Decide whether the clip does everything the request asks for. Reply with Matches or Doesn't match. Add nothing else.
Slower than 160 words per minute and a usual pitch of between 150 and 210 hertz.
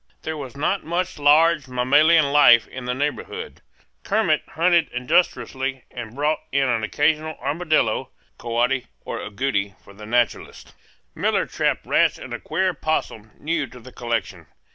Doesn't match